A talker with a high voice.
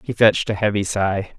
No: low, 100 Hz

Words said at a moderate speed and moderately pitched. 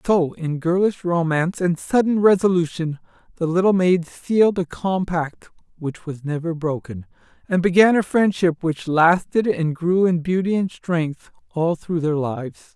Yes: average, 155 wpm; medium, 170 Hz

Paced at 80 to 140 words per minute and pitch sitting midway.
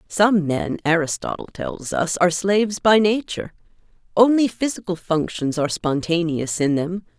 Yes: slow, 135 wpm; medium, 180 Hz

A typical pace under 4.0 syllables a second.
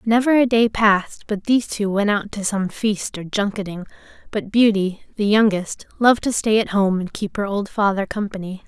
No: 5.1 syllables/s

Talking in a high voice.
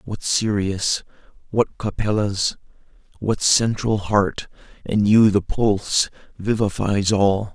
No: low, 105 Hz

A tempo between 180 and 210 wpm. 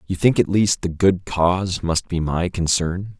Yes: fast, 205 wpm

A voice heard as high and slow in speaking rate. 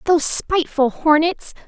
Yes: very high, 300 Hz; slow, 105 wpm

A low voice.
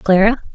No: high, 205 Hz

